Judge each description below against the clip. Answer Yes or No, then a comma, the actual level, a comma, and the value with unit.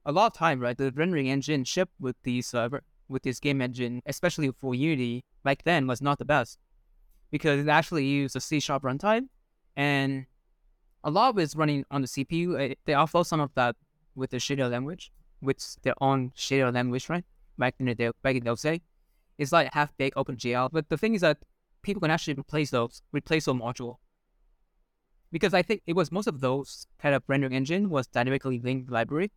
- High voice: No, medium, 140 Hz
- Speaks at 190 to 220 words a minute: Yes, average, 195 wpm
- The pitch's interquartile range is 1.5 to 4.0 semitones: Yes, average, 3.6 semitones